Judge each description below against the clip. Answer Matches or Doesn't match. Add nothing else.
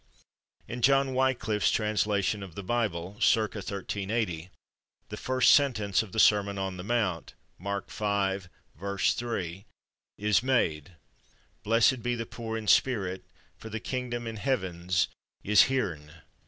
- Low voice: Matches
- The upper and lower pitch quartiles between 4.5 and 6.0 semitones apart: Doesn't match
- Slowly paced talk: Matches